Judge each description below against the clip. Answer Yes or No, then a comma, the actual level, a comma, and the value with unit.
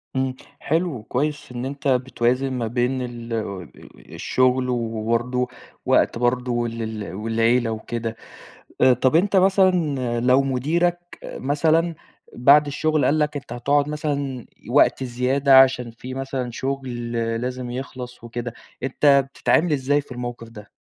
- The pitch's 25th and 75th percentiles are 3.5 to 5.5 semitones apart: No, average, 2.8 semitones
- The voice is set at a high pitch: No, low, 130 Hz